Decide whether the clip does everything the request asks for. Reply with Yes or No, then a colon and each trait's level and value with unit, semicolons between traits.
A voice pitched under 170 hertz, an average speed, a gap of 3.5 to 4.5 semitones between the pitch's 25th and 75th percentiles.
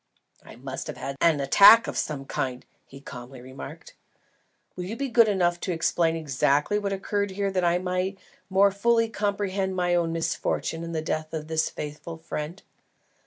No: medium, 175 Hz; average, 175 wpm; average, 4.1 semitones